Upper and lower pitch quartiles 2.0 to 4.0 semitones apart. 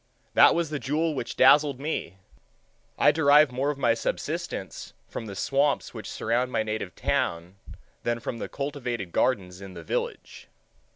No: average, 4.9 semitones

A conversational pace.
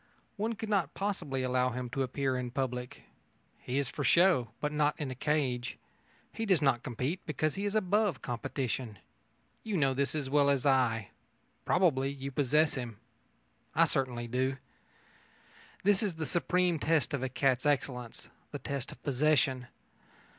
Yes: average, 160 wpm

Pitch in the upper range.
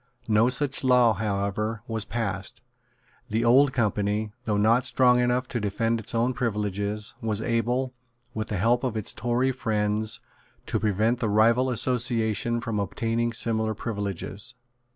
No: low, 115 Hz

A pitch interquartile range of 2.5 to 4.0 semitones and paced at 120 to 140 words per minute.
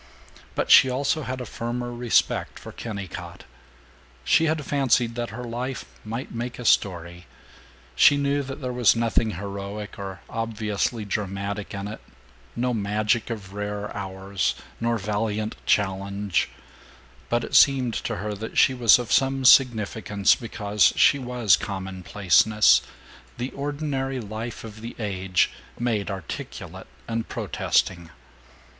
Yes: average, 3.5 semitones; slow, 135 wpm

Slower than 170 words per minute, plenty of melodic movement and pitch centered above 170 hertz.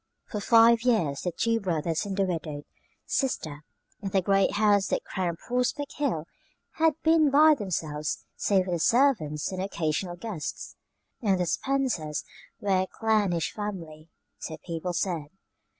Yes: average, 150 wpm; wide, 5.7 semitones; high, 190 Hz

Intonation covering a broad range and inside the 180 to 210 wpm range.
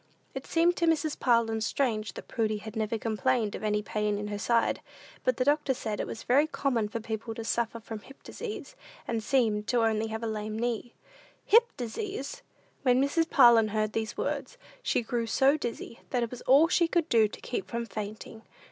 No: average, 3.7 semitones; average, 200 wpm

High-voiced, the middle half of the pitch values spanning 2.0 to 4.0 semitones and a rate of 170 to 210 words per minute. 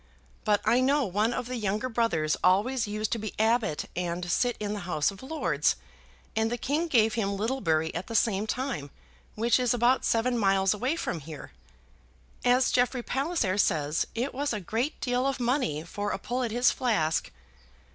No: high, 225 Hz; average, 4.6 semitones; average, 185 wpm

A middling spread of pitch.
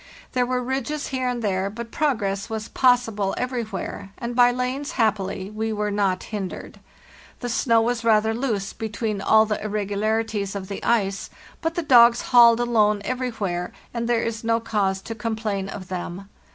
Yes: average, 3.1 semitones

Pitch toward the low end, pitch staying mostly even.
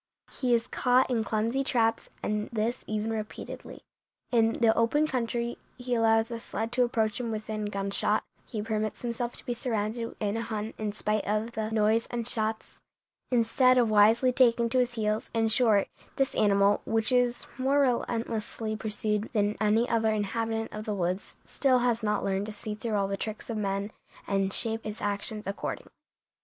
No: high, 225 Hz; narrow, 2.0 semitones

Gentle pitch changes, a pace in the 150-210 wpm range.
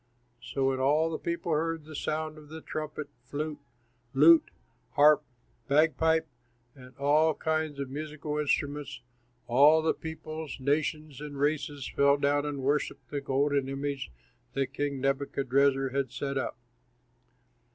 No: narrow, 2.0 semitones; average, 140 wpm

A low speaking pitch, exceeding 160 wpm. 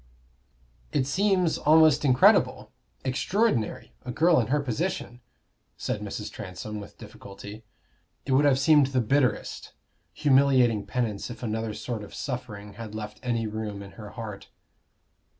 No: low, 120 Hz; slow, 135 wpm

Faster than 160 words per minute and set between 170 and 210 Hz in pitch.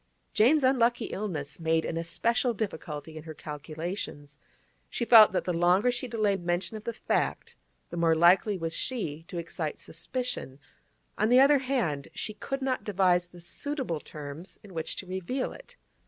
Yes: average, 170 wpm; medium, 185 Hz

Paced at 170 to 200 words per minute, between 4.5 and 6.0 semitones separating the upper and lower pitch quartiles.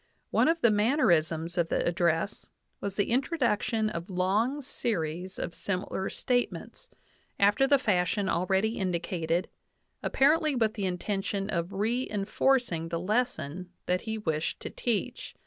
No: average, 145 wpm; average, 5.1 semitones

